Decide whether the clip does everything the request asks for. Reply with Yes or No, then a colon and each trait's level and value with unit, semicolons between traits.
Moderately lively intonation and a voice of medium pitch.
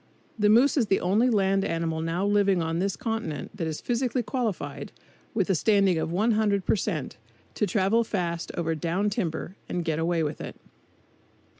No: average, 4.3 semitones; high, 195 Hz